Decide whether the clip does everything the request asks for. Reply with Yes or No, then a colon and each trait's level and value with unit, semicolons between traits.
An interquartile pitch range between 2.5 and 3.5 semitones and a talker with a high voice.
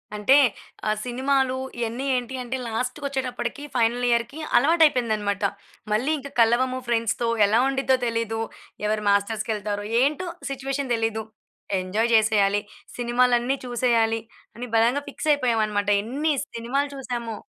Yes: average, 3.0 semitones; high, 240 Hz